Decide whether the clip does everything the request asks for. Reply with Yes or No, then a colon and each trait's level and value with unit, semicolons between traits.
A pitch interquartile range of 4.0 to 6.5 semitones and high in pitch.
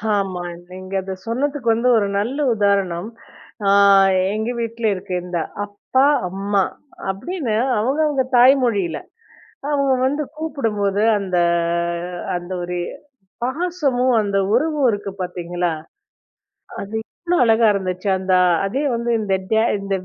Yes: average, 5.3 semitones; high, 210 Hz